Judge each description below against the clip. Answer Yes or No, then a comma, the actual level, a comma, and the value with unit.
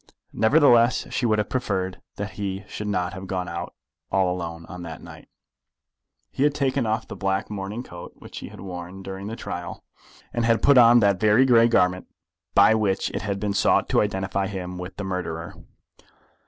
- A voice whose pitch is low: Yes, very low, 95 Hz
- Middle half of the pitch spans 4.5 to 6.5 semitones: No, average, 3.4 semitones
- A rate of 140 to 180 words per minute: No, average, 190 wpm